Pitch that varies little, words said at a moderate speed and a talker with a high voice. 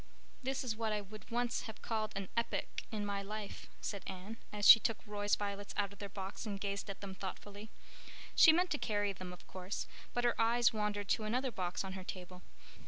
No: narrow, 2.3 semitones; fast, 215 wpm; high, 205 Hz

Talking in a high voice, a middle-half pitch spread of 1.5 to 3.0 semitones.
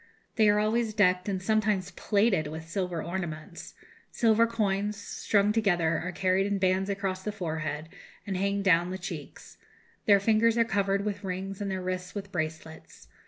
Yes: high, 195 Hz; narrow, 2.4 semitones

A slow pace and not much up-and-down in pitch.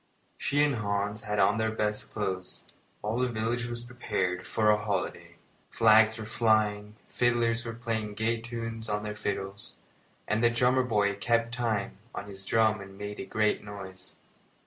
No: average, 170 wpm; narrow, 2.0 semitones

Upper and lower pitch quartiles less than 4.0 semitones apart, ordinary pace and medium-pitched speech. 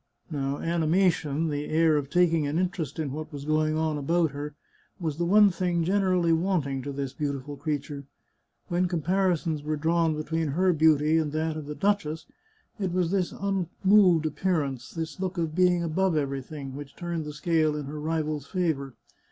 Yes: average, 3.0 semitones; average, 180 wpm; medium, 160 Hz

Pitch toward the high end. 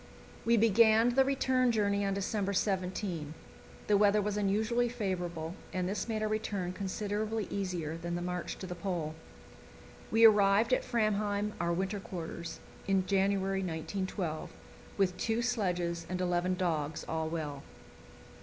Yes: high, 195 Hz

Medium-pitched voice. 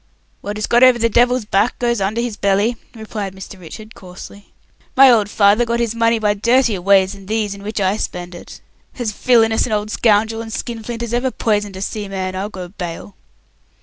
No: high, 215 Hz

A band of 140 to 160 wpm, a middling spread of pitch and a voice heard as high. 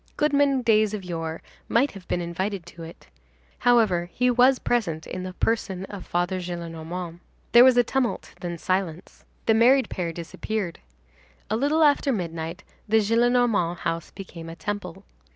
No: average, 155 wpm; wide, 5.7 semitones; high, 195 Hz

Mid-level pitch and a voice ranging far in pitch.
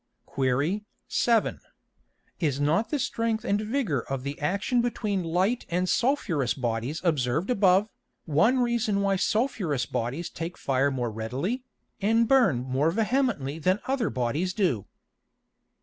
Yes: medium, 180 Hz; wide, 8.4 semitones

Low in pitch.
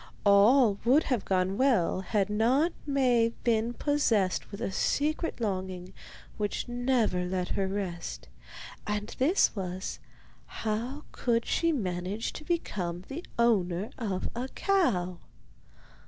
No: high, 215 Hz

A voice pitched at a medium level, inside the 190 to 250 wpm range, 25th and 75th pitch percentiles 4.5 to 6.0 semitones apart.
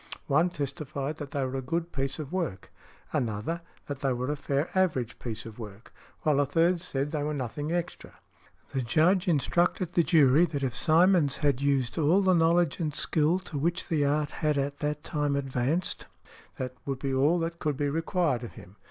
No: medium, 145 Hz; average, 200 wpm; average, 3.7 semitones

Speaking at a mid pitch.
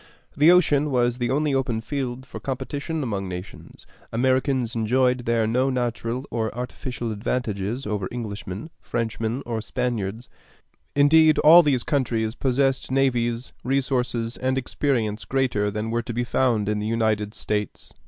No: low, 120 Hz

